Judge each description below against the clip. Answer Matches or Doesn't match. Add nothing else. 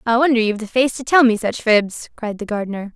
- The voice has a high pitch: Matches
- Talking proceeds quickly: Matches